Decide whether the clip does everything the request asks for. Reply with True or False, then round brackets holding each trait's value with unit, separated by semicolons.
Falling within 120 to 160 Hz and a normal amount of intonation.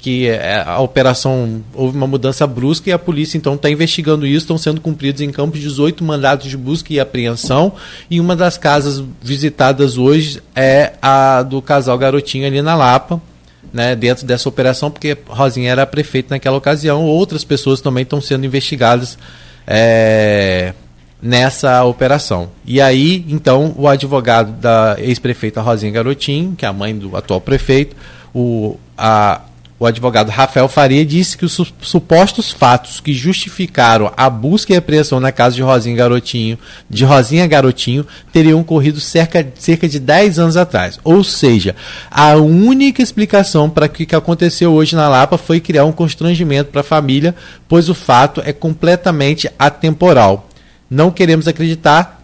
True (140 Hz; 4.3 semitones)